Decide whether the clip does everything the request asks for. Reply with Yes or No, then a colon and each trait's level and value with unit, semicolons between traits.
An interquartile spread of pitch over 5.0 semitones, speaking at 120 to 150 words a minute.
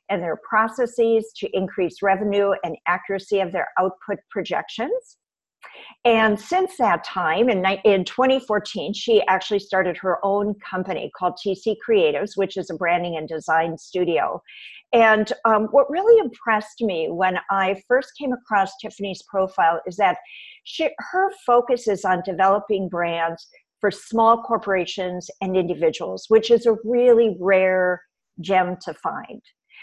No: average, 3.8 semitones; average, 140 wpm